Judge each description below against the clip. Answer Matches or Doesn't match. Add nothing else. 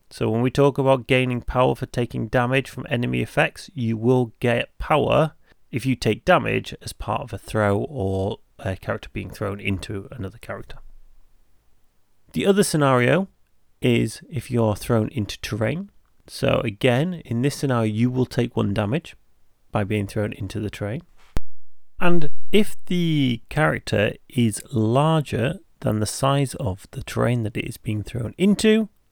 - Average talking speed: Matches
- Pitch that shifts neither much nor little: Matches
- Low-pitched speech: Matches